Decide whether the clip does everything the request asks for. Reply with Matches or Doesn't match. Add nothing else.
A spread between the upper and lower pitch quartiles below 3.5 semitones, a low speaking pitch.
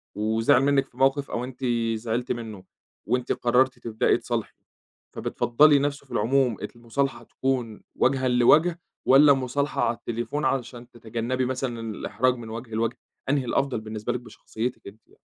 Matches